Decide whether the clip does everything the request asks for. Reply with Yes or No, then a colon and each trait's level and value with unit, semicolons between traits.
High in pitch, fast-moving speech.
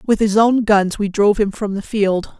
Yes: high, 205 Hz; fast, 250 wpm